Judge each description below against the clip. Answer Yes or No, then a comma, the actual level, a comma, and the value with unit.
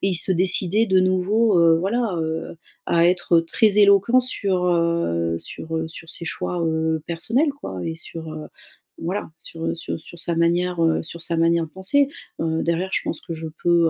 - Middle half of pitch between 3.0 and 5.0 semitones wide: No, narrow, 2.6 semitones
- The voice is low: No, medium, 170 Hz